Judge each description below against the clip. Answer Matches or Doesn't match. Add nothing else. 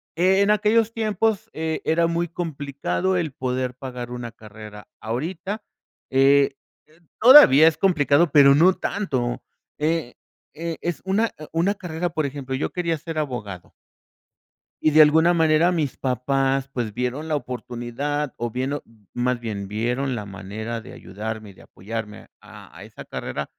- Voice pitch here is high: Doesn't match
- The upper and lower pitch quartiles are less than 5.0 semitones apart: Doesn't match